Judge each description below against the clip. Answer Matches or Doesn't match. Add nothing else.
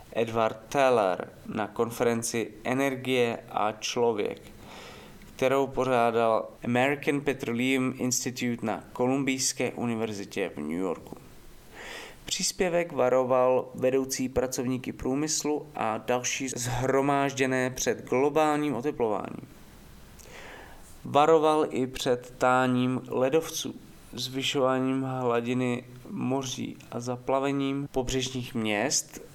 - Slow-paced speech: Matches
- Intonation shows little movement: Matches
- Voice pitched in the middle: Doesn't match